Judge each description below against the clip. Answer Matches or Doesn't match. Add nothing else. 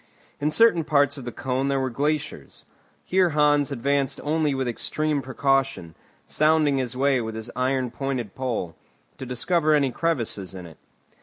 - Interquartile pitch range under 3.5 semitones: Matches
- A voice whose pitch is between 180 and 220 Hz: Doesn't match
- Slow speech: Doesn't match